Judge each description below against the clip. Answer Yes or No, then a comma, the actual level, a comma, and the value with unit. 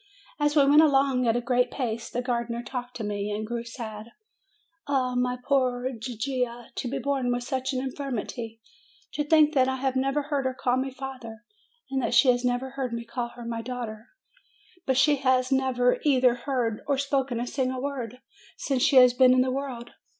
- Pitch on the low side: No, very high, 255 Hz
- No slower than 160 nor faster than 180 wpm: No, average, 200 wpm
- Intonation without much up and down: Yes, narrow, 2.0 semitones